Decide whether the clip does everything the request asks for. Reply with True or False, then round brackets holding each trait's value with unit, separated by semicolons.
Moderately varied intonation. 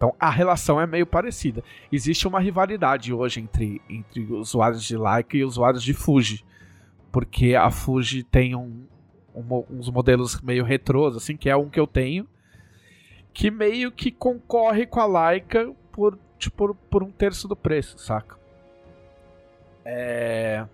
False (7.2 semitones)